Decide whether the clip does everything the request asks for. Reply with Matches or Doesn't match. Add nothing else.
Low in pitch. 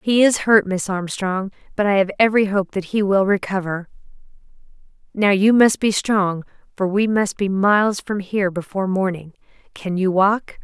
Doesn't match